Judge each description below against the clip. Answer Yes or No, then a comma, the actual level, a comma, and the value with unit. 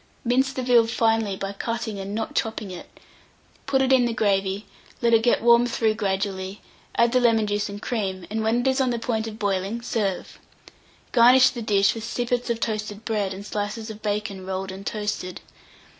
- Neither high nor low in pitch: No, high, 220 Hz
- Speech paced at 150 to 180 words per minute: No, average, 195 wpm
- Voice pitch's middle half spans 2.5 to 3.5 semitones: Yes, average, 2.9 semitones